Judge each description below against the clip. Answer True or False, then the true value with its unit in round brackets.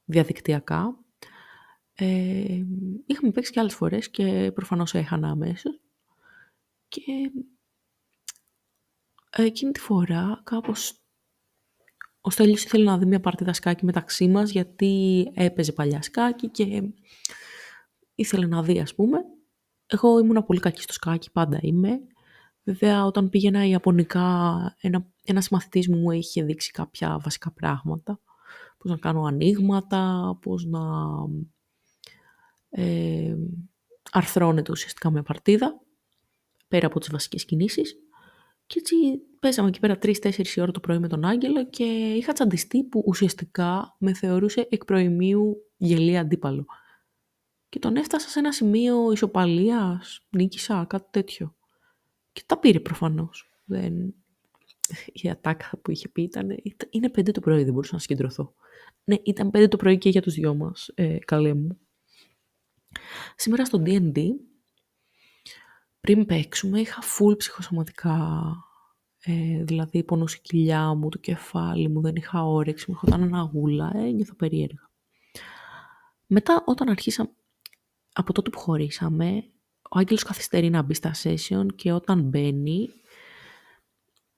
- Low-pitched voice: False (190 Hz)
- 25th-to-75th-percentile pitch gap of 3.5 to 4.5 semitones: False (5.0 semitones)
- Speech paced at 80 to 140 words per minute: True (130 wpm)